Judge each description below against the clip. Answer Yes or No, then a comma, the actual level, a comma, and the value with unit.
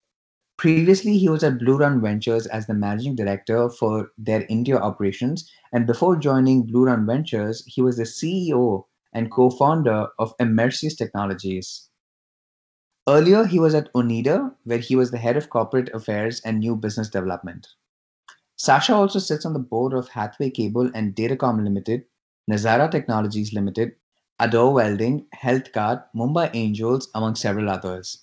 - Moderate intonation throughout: Yes, average, 3.5 semitones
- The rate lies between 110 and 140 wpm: No, average, 150 wpm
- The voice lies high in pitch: No, low, 120 Hz